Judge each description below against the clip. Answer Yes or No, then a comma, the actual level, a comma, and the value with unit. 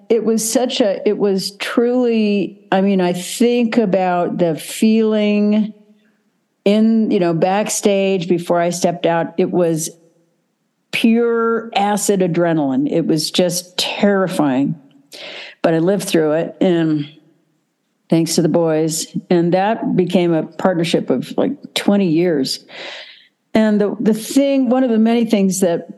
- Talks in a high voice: Yes, high, 200 Hz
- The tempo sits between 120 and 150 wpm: Yes, average, 140 wpm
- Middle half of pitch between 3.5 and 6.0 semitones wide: Yes, average, 4.4 semitones